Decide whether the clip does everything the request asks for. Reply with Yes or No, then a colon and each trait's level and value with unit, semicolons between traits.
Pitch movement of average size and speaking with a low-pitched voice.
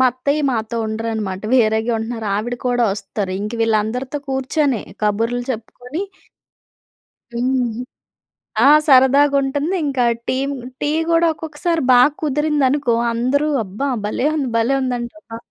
No: average, 3.8 semitones; very high, 250 Hz